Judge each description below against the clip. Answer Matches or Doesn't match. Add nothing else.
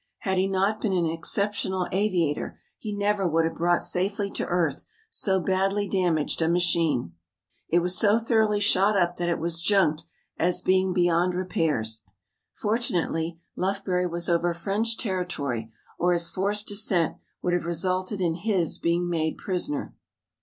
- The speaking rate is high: Doesn't match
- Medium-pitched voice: Matches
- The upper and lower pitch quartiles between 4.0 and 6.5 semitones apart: Doesn't match